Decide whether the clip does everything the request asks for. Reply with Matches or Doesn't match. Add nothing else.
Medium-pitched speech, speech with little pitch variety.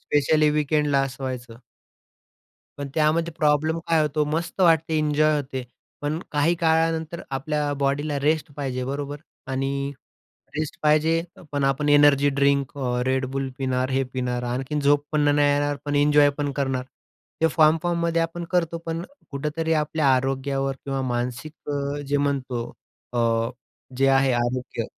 Matches